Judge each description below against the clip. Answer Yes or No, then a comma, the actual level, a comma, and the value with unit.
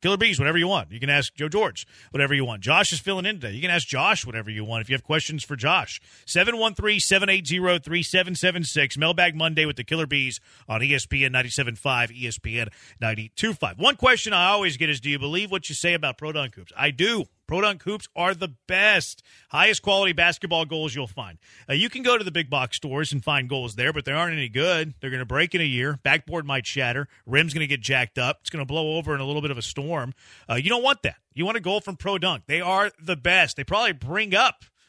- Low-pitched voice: No, medium, 155 Hz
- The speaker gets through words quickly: Yes, fast, 235 wpm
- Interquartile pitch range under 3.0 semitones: No, average, 5.2 semitones